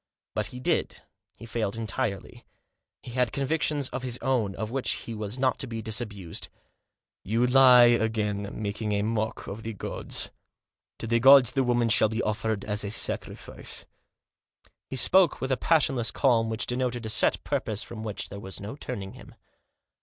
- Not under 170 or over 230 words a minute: Yes, average, 175 wpm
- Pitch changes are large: No, average, 3.0 semitones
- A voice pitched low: Yes, low, 115 Hz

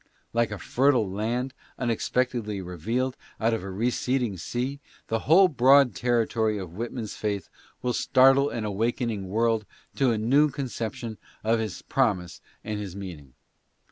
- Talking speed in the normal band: Yes, average, 145 wpm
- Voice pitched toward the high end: No, low, 115 Hz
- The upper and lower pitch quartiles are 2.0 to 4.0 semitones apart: Yes, average, 3.4 semitones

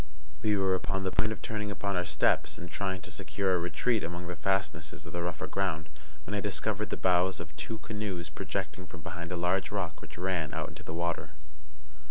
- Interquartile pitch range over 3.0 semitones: No, narrow, 2.5 semitones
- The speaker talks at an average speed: No, fast, 215 wpm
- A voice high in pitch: No, very low, 95 Hz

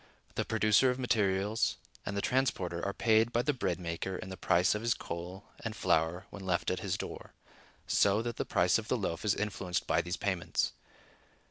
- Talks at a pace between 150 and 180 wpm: No, average, 200 wpm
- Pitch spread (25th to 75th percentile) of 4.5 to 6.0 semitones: No, average, 3.8 semitones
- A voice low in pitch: Yes, low, 100 Hz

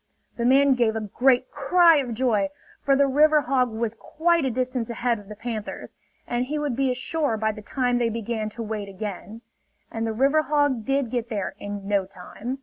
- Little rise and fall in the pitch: No, average, 3.9 semitones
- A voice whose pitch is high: Yes, high, 240 Hz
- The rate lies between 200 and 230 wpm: Yes, fast, 205 wpm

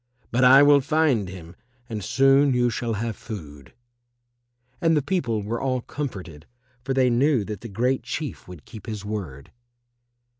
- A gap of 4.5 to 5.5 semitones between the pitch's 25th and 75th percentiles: Yes, average, 5.1 semitones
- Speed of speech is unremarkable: Yes, average, 160 wpm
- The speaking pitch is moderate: No, low, 120 Hz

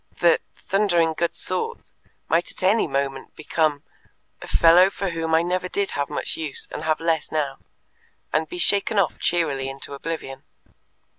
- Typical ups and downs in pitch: Yes, average, 3.4 semitones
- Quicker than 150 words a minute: Yes, average, 160 wpm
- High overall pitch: No, medium, 165 Hz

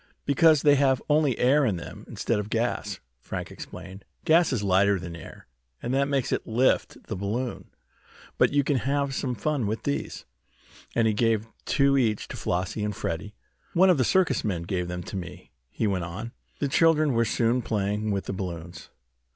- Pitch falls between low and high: No, low, 115 Hz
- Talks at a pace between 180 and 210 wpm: Yes, average, 190 wpm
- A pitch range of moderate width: No, wide, 5.9 semitones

